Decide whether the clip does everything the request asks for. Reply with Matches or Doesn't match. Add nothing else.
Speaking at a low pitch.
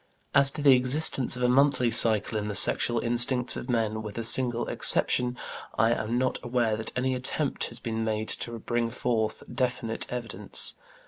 Matches